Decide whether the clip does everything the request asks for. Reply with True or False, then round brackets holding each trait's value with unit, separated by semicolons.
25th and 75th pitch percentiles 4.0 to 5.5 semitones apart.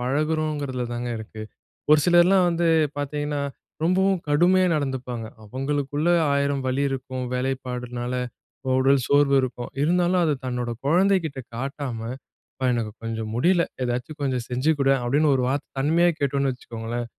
False (3.6 semitones)